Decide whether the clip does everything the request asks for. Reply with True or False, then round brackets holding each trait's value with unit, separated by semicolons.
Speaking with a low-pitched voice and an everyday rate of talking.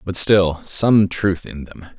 True (95 Hz; 150 wpm)